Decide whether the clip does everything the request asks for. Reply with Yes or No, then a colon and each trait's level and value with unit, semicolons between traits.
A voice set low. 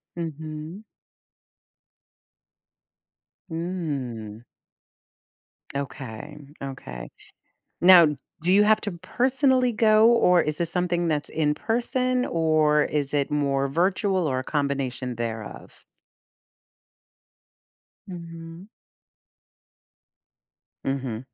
No: medium, 160 Hz